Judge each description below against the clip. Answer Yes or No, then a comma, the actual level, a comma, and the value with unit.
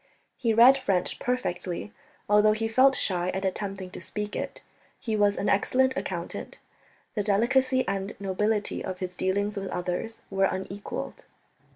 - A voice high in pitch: Yes, high, 205 Hz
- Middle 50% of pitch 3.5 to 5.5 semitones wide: No, average, 2.8 semitones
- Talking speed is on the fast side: No, average, 150 wpm